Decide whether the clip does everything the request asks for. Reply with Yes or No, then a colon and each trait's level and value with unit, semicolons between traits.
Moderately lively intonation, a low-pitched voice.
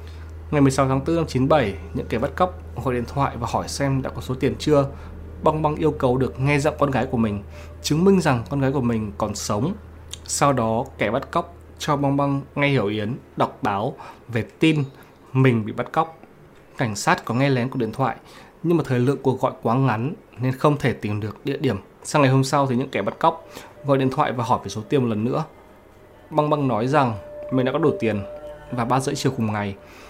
Yes: average, 4.5 semitones; low, 130 Hz